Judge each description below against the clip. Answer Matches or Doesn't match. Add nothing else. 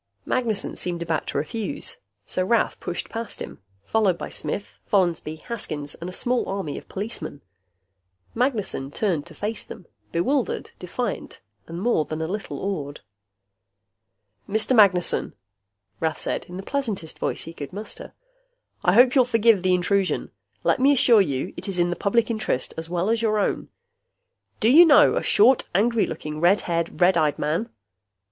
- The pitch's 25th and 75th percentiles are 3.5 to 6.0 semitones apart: Matches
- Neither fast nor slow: Matches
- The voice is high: Matches